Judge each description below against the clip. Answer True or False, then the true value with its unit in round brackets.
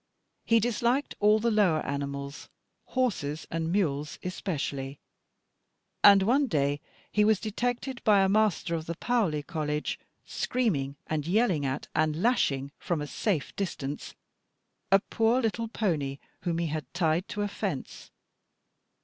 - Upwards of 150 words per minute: False (140 wpm)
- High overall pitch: False (175 Hz)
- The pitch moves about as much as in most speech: False (6.6 semitones)